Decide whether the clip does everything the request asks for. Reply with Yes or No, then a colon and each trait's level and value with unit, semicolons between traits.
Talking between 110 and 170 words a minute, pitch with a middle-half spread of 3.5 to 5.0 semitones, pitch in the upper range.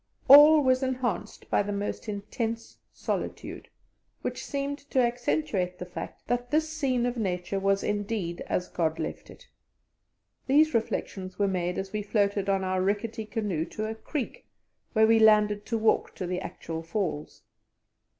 Yes: average, 160 wpm; average, 4.6 semitones; high, 210 Hz